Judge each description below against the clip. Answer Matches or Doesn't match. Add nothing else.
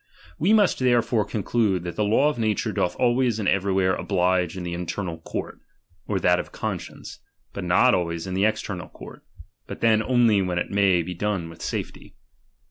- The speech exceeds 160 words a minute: Matches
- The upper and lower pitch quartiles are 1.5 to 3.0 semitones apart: Doesn't match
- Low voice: Matches